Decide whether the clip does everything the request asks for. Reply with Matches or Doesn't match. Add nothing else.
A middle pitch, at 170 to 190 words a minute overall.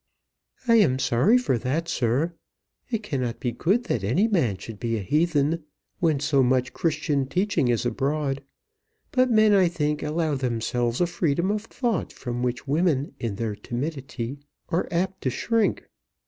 Doesn't match